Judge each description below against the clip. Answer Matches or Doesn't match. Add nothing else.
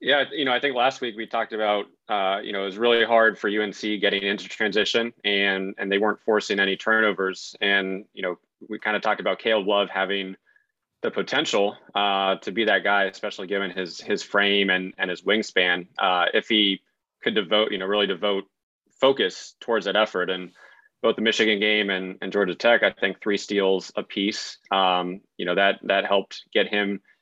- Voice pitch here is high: Doesn't match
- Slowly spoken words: Doesn't match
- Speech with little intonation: Matches